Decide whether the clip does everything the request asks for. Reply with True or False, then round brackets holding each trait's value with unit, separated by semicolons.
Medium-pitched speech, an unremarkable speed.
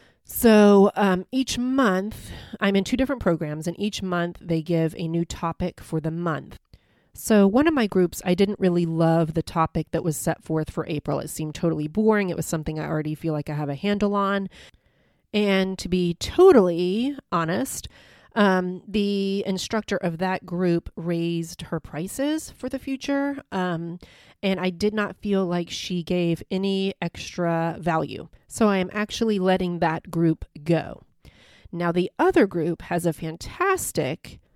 True (180 Hz; 170 wpm)